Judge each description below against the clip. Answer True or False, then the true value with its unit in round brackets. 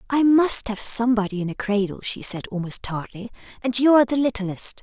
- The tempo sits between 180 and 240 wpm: True (200 wpm)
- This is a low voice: False (225 Hz)